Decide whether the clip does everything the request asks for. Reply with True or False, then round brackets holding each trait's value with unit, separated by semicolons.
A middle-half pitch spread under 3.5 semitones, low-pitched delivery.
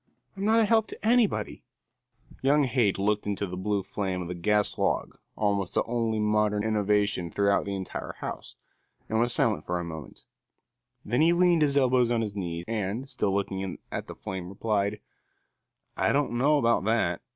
False (4.3 semitones; 105 Hz)